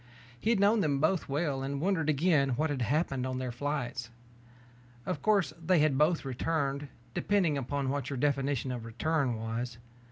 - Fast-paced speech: No, average, 170 wpm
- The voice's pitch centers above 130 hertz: Yes, medium, 140 Hz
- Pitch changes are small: No, average, 3.6 semitones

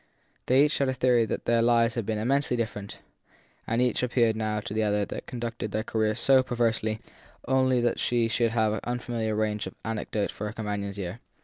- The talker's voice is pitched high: No, low, 115 Hz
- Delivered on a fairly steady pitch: Yes, narrow, 2.2 semitones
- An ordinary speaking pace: No, fast, 210 wpm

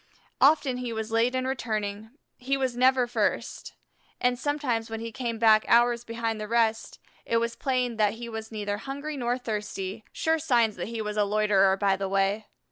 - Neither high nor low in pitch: No, high, 230 Hz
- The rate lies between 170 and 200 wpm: Yes, average, 190 wpm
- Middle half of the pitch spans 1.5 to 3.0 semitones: Yes, average, 2.7 semitones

